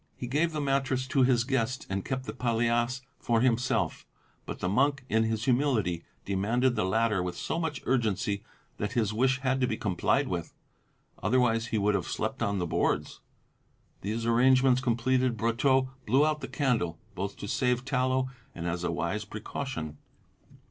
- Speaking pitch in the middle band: No, low, 120 Hz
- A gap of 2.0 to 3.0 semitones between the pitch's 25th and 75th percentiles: No, average, 3.9 semitones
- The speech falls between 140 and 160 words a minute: No, average, 170 wpm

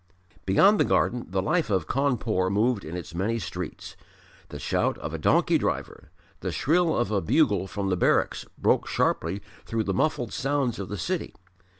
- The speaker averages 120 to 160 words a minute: No, average, 180 wpm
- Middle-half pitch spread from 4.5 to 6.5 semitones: Yes, average, 5.2 semitones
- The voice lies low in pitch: Yes, low, 105 Hz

